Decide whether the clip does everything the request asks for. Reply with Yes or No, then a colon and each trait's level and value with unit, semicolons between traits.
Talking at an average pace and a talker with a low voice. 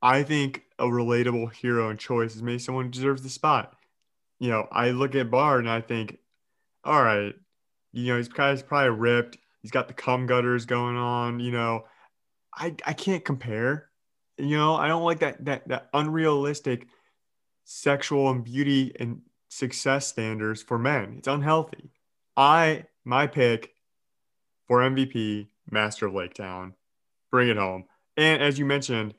Yes: average, 160 wpm; low, 125 Hz